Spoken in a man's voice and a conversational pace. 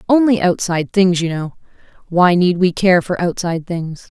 No: female; average, 170 wpm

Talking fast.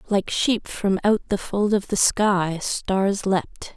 No: average, 175 wpm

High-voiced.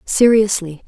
Yes: high, 200 Hz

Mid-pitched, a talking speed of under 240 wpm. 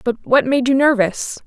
No: very high, 250 Hz; fast, 205 wpm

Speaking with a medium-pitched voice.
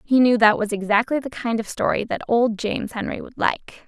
No: high, 230 Hz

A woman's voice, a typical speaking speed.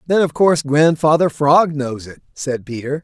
No: male; average, 180 wpm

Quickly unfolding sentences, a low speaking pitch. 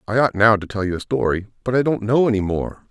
Yes: fast, 290 wpm; low, 110 Hz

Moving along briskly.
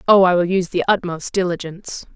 No: average, 195 wpm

